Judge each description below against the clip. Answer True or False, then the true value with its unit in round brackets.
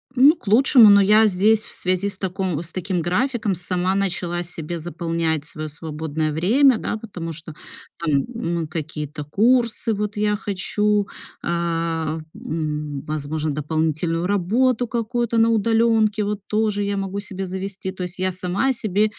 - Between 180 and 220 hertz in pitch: True (185 Hz)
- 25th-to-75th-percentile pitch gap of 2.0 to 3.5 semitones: False (4.5 semitones)